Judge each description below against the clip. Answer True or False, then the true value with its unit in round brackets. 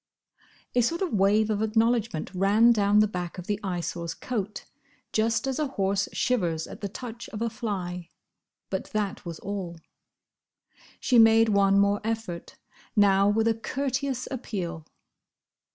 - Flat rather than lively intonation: False (3.0 semitones)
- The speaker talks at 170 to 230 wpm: False (150 wpm)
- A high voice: True (210 Hz)